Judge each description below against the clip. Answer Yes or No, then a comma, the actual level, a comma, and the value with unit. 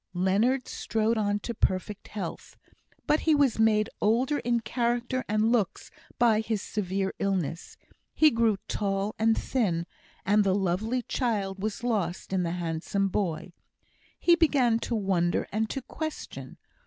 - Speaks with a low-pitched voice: No, high, 215 Hz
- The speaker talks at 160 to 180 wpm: No, average, 145 wpm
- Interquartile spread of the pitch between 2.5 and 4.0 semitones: Yes, average, 3.6 semitones